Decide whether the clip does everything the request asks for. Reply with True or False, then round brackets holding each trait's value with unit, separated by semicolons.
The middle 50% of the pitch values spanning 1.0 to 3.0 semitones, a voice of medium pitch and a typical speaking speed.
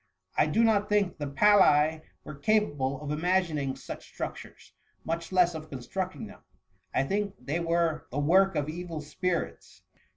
False (4.3 semitones; 165 Hz; 160 wpm)